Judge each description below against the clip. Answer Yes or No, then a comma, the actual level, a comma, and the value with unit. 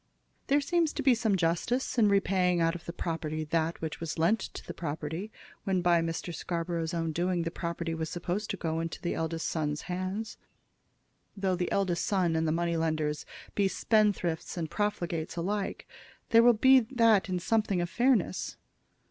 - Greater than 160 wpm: Yes, average, 180 wpm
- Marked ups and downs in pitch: No, average, 3.7 semitones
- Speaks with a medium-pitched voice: Yes, medium, 175 Hz